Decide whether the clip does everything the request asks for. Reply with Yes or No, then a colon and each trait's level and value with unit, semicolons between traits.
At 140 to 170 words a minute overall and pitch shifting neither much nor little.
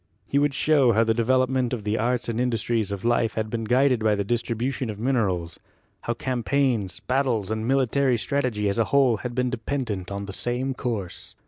No: average, 200 wpm; average, 3.0 semitones